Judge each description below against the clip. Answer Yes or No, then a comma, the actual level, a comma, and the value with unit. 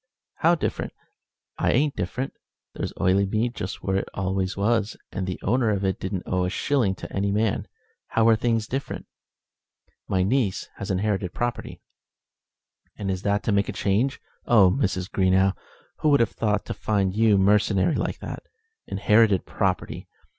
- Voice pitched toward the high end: No, low, 100 Hz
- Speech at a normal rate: Yes, average, 160 wpm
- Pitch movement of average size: Yes, average, 3.1 semitones